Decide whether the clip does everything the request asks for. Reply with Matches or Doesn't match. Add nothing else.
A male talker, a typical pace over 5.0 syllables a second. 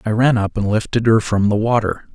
Matches